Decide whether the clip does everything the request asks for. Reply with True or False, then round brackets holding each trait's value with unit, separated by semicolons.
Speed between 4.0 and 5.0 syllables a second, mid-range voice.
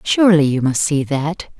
True (4.9 syllables/s; 155 Hz)